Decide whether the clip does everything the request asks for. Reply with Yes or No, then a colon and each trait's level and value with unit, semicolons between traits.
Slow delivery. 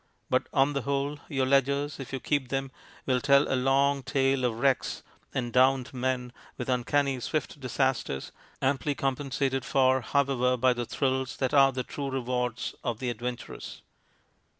No: average, 160 wpm